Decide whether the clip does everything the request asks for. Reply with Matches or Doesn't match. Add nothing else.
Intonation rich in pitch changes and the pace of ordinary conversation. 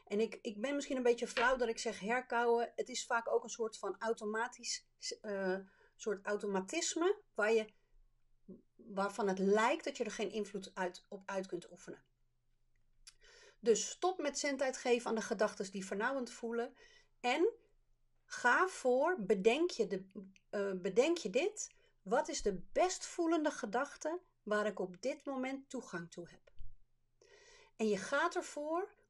Matches